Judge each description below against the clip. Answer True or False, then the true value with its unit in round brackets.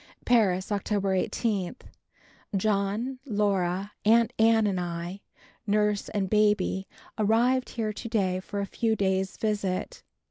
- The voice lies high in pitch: True (205 Hz)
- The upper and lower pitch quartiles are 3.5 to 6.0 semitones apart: False (2.5 semitones)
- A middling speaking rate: False (120 wpm)